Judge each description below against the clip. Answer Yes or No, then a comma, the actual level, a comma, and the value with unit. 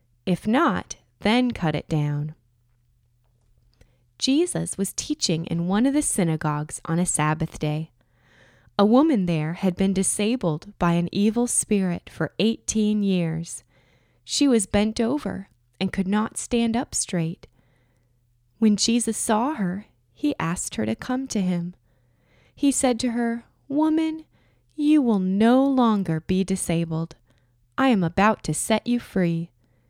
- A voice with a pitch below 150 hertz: No, medium, 180 Hz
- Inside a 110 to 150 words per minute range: Yes, average, 140 wpm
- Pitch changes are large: Yes, wide, 7.3 semitones